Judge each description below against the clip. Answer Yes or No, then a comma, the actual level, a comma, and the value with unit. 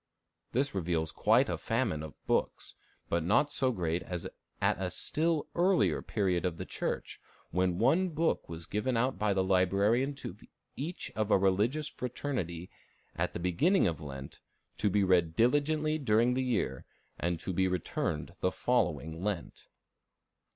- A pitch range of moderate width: No, wide, 7.2 semitones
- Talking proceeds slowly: No, average, 160 wpm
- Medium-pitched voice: No, low, 100 Hz